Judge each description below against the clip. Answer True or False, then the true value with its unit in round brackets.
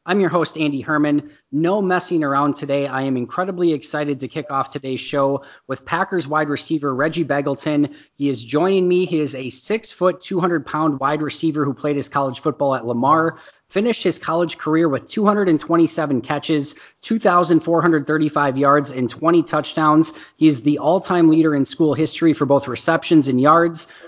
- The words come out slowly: False (175 wpm)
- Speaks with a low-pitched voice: False (155 Hz)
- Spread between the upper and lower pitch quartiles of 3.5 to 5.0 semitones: False (2.9 semitones)